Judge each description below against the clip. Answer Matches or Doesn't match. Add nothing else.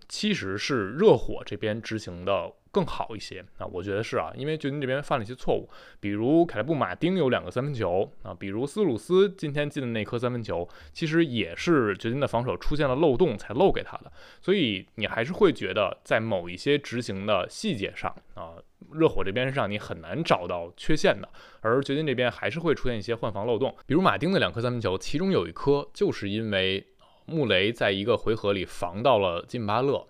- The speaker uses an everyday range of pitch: Doesn't match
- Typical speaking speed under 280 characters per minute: Doesn't match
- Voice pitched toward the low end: Matches